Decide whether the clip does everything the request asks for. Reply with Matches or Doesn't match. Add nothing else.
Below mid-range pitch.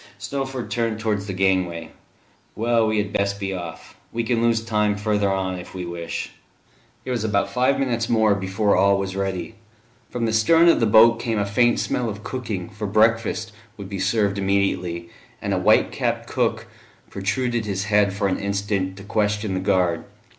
Matches